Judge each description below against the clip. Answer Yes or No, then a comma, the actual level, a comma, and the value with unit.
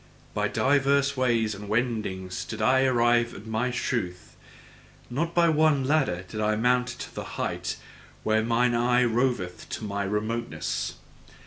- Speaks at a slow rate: No, average, 145 wpm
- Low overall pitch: Yes, low, 120 Hz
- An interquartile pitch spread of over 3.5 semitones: No, average, 3.2 semitones